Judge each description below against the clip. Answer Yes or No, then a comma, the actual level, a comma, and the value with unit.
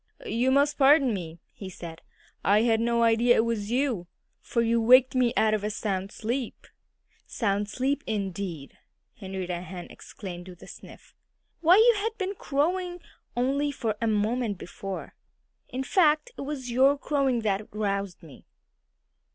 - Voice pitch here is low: No, high, 230 Hz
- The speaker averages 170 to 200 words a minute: No, average, 155 wpm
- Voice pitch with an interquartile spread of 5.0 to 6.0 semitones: Yes, wide, 5.6 semitones